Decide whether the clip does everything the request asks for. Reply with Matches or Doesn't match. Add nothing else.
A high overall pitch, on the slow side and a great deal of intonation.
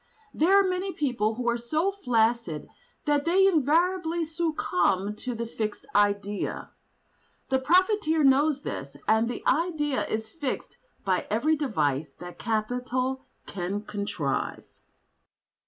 Matches